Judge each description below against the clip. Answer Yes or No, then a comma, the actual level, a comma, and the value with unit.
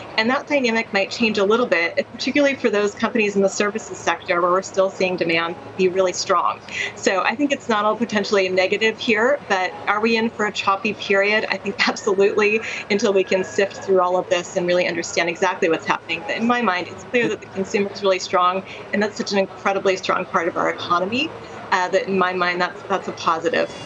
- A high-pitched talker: Yes, high, 195 Hz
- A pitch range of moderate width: Yes, average, 3.0 semitones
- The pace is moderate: No, fast, 225 wpm